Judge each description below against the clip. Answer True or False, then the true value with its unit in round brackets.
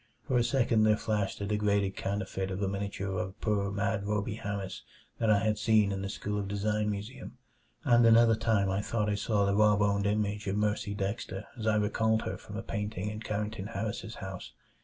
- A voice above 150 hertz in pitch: False (105 Hz)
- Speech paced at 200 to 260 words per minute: True (205 wpm)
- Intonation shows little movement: True (1.4 semitones)